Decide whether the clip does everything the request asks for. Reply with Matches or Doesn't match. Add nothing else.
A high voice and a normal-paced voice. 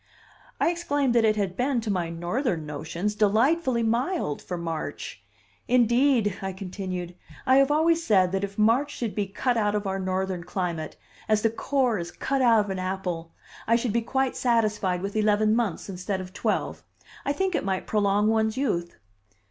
Matches